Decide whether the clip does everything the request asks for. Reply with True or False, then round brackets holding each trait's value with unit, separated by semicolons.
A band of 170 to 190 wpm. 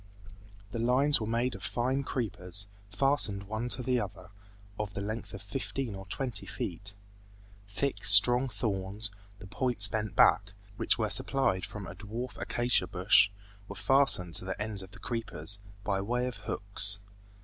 False (160 wpm)